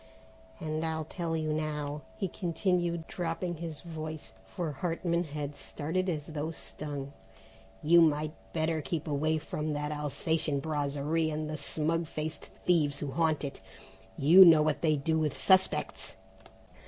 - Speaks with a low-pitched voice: No, medium, 155 Hz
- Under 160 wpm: Yes, average, 145 wpm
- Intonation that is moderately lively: No, narrow, 1.9 semitones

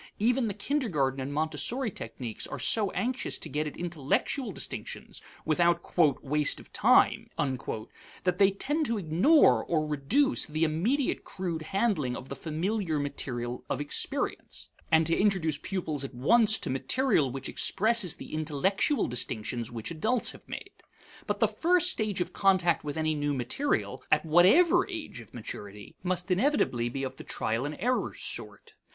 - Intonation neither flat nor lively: No, wide, 7.6 semitones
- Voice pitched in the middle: Yes, medium, 165 Hz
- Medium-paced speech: Yes, average, 160 wpm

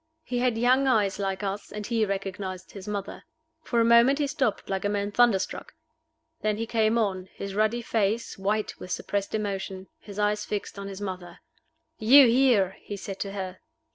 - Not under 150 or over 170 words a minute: No, average, 185 wpm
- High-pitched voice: Yes, high, 205 Hz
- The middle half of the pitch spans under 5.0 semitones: Yes, average, 2.8 semitones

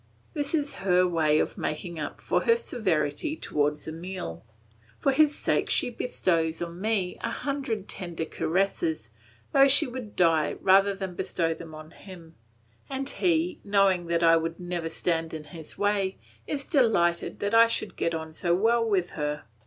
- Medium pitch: Yes, medium, 180 Hz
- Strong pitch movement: Yes, wide, 5.8 semitones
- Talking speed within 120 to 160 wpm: No, average, 170 wpm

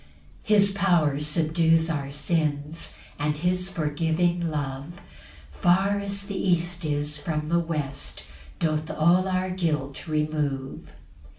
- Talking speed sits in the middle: No, slow, 120 wpm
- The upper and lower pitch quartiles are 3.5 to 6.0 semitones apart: No, average, 3.1 semitones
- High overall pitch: No, medium, 160 Hz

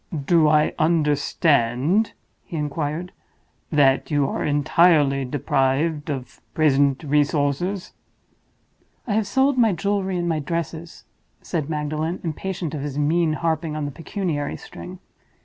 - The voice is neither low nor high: Yes, medium, 155 Hz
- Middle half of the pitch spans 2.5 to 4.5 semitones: Yes, average, 3.1 semitones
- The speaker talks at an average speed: No, slow, 125 wpm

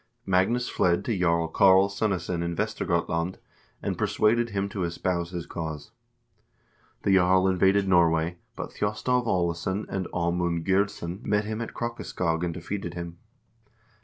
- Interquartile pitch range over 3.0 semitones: No, average, 2.7 semitones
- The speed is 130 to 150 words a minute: Yes, slow, 135 wpm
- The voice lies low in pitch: Yes, very low, 90 Hz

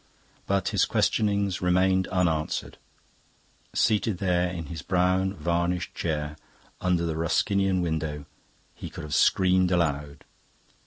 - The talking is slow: Yes, slow, 115 wpm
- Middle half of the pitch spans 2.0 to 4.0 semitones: Yes, narrow, 2.6 semitones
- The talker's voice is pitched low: Yes, very low, 90 Hz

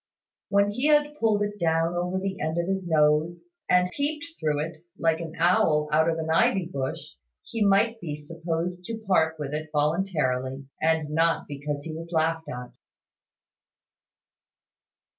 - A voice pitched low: No, medium, 165 Hz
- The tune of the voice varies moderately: Yes, average, 3.8 semitones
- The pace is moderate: Yes, average, 160 wpm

